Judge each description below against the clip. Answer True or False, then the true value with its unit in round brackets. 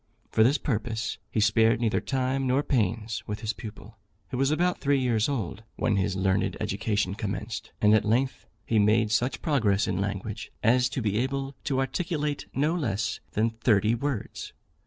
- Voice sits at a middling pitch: False (115 Hz)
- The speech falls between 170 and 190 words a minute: True (175 wpm)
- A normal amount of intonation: True (4.0 semitones)